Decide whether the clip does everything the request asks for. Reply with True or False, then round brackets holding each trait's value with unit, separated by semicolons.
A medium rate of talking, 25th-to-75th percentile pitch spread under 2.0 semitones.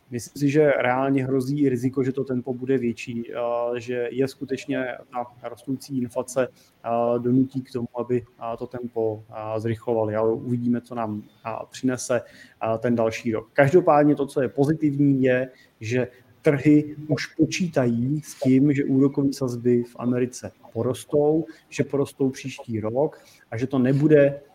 False (140 wpm; 2.6 semitones)